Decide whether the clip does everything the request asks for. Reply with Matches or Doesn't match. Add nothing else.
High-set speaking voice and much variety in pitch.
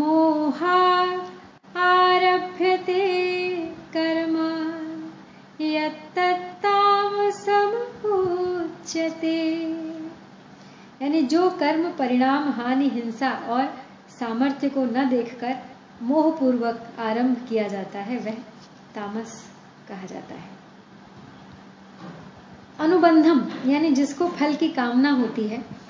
Matches